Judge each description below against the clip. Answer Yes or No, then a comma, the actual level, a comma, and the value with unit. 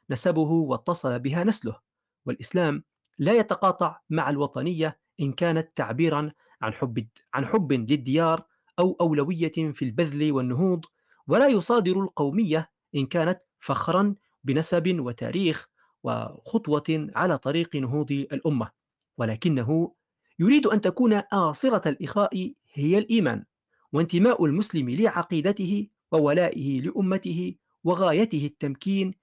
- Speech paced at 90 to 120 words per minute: Yes, average, 105 wpm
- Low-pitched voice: No, medium, 165 Hz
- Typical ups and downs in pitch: Yes, average, 4.6 semitones